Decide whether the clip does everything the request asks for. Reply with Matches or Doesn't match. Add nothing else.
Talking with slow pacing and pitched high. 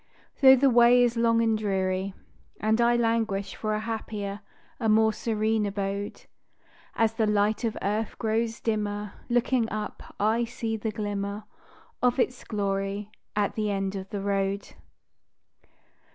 Doesn't match